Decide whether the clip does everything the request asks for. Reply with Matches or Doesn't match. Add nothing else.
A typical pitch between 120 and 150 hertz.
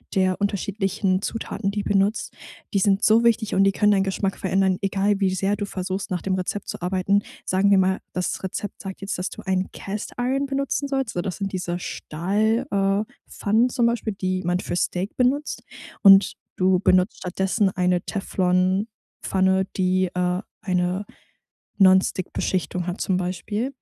Doesn't match